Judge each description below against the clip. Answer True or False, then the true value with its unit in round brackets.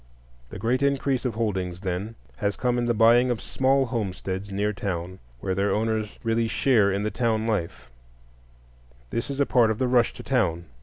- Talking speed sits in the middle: True (190 wpm)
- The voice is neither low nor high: False (110 Hz)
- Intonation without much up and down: False (3.7 semitones)